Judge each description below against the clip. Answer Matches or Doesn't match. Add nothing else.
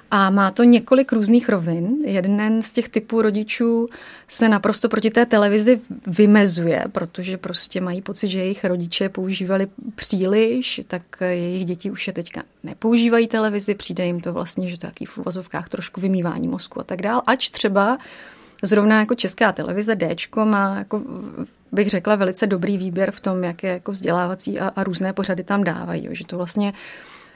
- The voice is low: Doesn't match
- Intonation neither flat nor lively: Matches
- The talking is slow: Doesn't match